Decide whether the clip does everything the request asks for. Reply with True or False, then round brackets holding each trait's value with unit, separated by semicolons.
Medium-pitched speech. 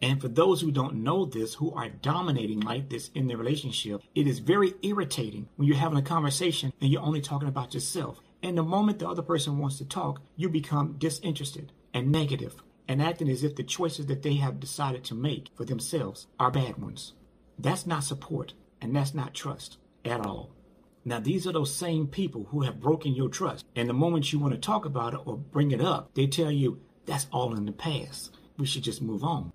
True (145 Hz)